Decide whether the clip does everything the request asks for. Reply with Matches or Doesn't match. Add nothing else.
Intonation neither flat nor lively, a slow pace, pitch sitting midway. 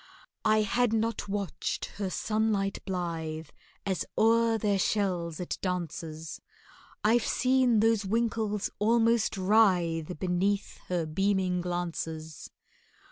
Doesn't match